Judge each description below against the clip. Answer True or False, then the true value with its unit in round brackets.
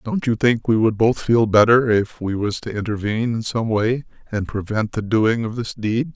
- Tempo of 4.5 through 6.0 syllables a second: True (4.9 syllables/s)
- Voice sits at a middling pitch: False (110 Hz)